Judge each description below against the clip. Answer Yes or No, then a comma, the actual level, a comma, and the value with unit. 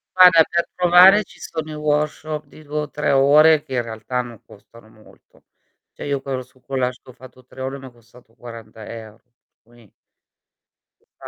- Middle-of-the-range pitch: No, low, 130 Hz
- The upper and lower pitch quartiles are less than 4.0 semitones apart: No, average, 4.3 semitones